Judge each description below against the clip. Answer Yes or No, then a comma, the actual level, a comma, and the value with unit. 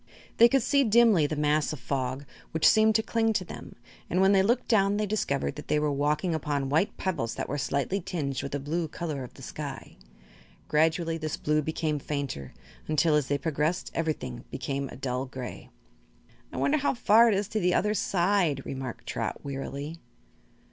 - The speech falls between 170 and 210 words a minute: Yes, average, 190 wpm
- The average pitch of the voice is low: No, medium, 155 Hz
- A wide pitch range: Yes, wide, 5.8 semitones